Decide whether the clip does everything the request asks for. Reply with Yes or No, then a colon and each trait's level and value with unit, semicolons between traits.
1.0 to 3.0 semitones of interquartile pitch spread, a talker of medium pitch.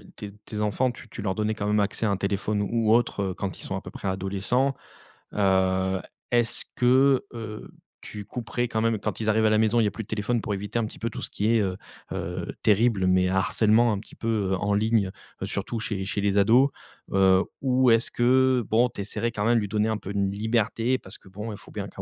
No: narrow, 2.6 semitones; low, 105 Hz